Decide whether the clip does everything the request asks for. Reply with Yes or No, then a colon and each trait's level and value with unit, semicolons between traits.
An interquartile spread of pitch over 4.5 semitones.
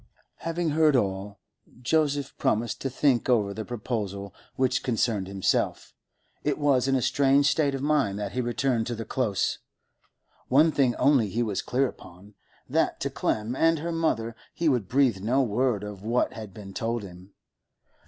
Yes: average, 4.9 semitones